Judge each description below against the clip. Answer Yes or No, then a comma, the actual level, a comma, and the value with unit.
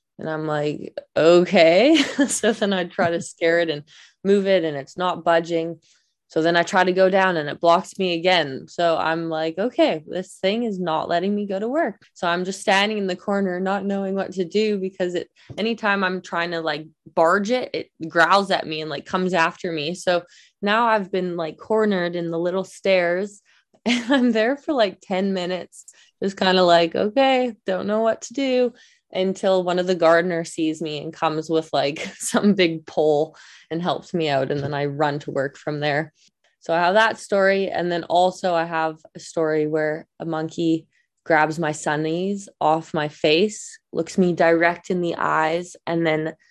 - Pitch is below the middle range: No, medium, 175 Hz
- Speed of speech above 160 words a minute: Yes, average, 200 wpm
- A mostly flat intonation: No, average, 3.5 semitones